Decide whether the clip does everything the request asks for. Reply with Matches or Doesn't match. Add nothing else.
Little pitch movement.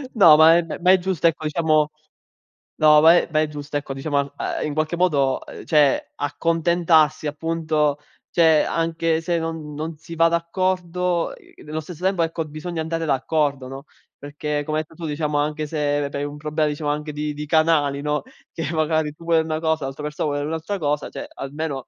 Matches